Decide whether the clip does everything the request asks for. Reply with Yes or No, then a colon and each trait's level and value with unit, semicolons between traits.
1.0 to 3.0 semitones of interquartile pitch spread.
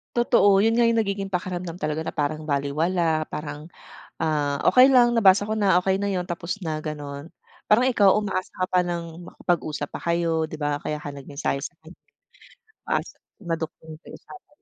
No: average, 4.4 semitones